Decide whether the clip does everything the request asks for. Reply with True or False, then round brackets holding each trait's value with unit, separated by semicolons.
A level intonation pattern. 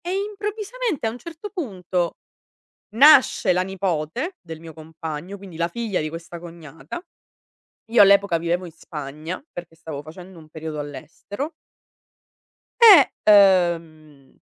False (6.5 semitones)